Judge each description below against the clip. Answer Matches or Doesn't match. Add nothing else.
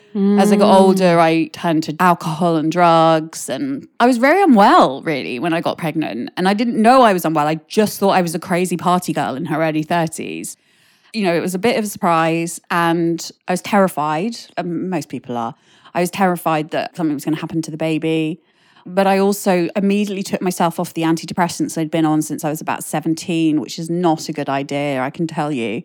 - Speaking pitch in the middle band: Matches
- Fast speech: Matches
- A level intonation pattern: Doesn't match